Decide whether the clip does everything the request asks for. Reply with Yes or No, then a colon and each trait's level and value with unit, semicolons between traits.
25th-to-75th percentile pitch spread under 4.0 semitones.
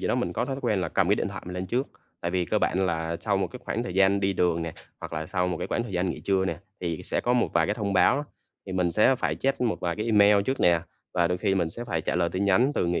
Yes: average, 3.4 semitones